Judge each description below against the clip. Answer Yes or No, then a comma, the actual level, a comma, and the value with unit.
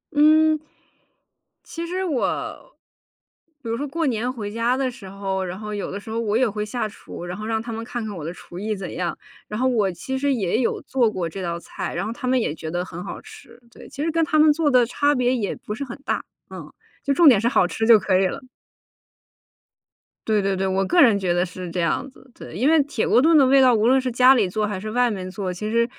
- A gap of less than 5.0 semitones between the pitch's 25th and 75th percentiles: No, average, 5.3 semitones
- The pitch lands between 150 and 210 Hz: No, high, 225 Hz